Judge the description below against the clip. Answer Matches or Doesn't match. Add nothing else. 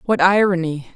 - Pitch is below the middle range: Doesn't match